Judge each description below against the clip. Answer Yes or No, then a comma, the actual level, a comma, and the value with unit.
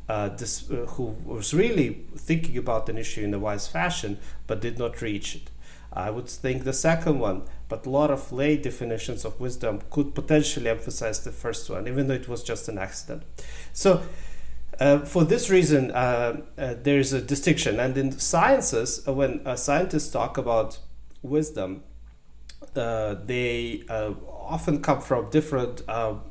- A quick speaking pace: Yes, fast, 170 wpm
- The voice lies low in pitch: Yes, low, 125 Hz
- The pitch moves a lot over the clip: No, average, 4.5 semitones